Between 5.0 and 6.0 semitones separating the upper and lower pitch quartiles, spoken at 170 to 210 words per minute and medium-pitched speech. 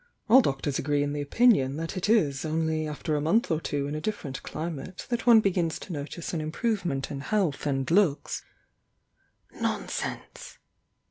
Yes: average, 5.3 semitones; average, 180 wpm; medium, 155 Hz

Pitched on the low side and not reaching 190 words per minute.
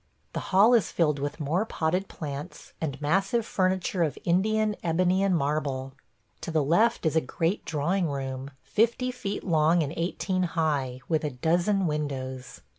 No: medium, 165 Hz; average, 160 wpm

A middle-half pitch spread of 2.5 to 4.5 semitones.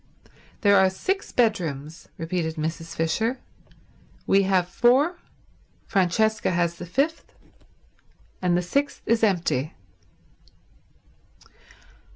No: average, 5.2 semitones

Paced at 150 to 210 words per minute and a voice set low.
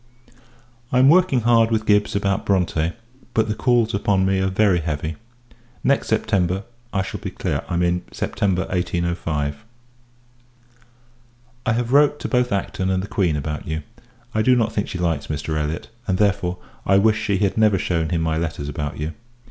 Yes: average, 180 wpm; very low, 95 Hz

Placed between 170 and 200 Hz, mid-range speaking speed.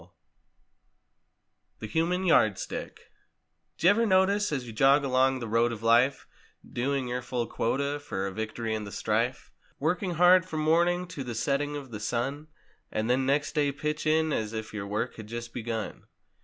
No: low, 130 Hz; average, 175 wpm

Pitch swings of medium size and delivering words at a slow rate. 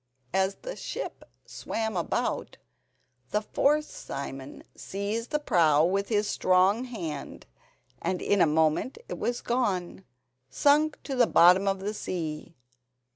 No: wide, 6.2 semitones; slow, 130 wpm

